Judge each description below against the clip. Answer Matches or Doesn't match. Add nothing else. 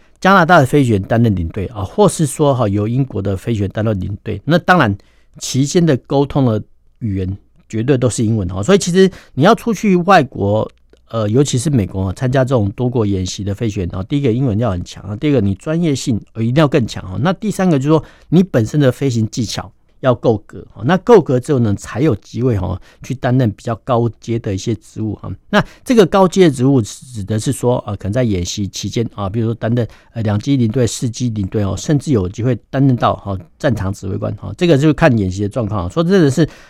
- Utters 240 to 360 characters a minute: Matches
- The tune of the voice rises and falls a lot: Matches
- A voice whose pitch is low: Matches